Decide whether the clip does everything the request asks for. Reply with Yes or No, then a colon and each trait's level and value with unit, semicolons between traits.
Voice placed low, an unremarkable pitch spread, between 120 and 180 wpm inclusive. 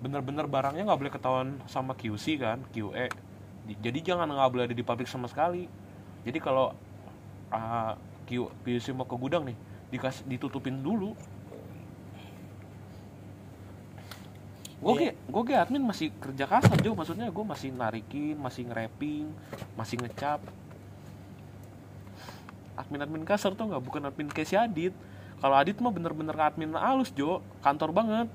No: low, 125 Hz; wide, 6.2 semitones; average, 130 wpm